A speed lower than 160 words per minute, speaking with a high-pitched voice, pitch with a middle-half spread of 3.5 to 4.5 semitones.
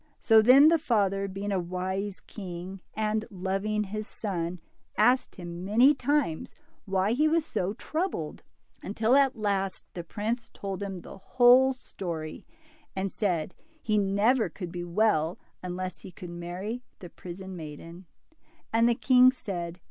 Yes: average, 150 wpm; high, 195 Hz; average, 4.0 semitones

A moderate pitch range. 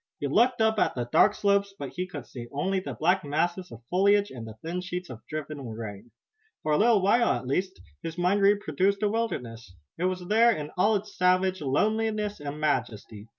No: wide, 6.3 semitones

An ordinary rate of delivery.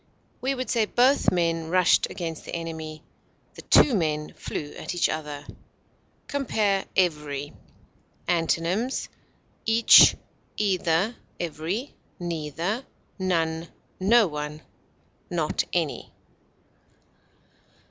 No: slow, 95 wpm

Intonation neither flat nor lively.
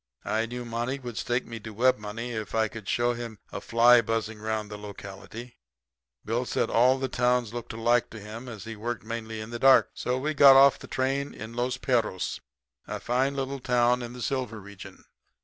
No: narrow, 2.1 semitones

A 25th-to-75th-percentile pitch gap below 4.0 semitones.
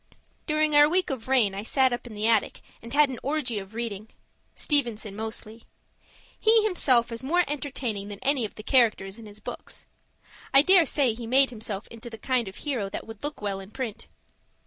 No: average, 4.5 semitones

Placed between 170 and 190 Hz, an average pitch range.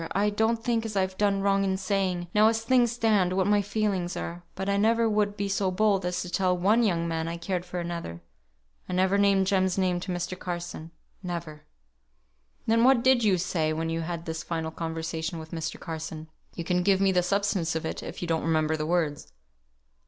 Yes: medium, 185 Hz; average, 3.2 semitones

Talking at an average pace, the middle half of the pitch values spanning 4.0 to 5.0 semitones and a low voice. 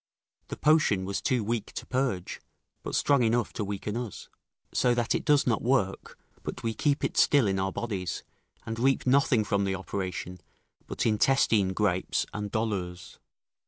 Yes: average, 165 wpm; average, 4.4 semitones; low, 110 Hz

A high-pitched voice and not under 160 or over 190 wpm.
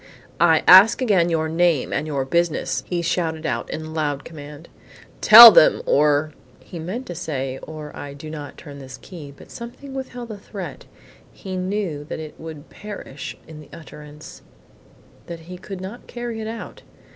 No: medium, 160 Hz; average, 175 wpm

